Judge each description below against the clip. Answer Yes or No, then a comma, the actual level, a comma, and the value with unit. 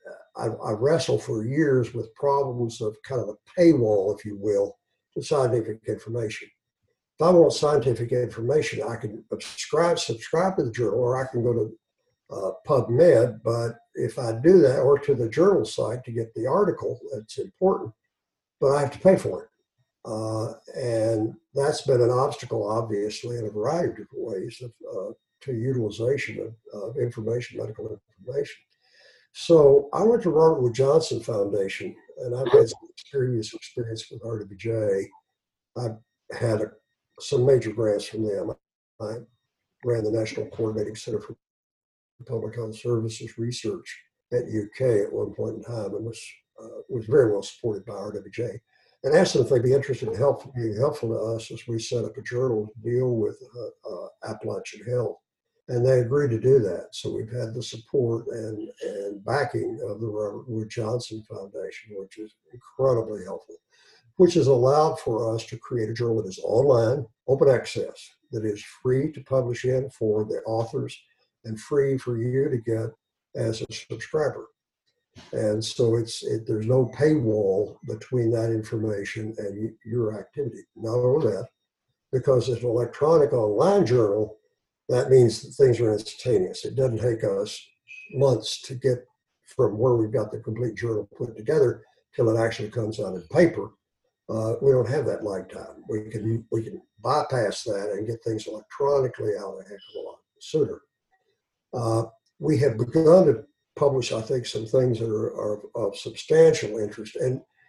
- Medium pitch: No, low, 125 Hz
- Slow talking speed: No, average, 170 wpm